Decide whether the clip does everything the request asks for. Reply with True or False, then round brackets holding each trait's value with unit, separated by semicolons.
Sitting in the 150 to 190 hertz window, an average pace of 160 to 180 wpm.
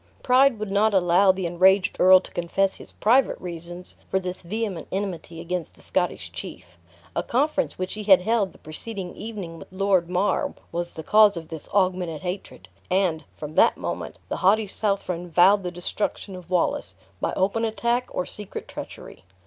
True (185 Hz; 175 wpm)